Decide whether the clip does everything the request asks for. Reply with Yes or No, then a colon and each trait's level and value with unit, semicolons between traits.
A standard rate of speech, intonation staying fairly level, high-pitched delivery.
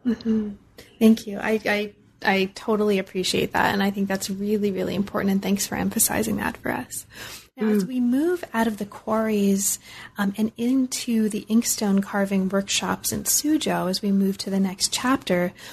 Yes: average, 180 wpm; narrow, 2.2 semitones; high, 205 Hz